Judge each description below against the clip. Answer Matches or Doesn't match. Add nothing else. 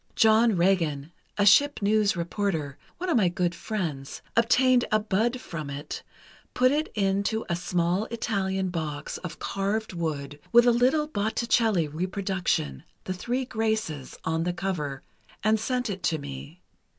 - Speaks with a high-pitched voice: Matches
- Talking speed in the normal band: Matches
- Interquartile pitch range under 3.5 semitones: Doesn't match